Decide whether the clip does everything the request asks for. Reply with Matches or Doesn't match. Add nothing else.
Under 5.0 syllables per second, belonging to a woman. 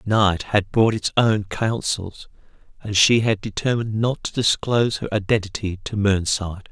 Doesn't match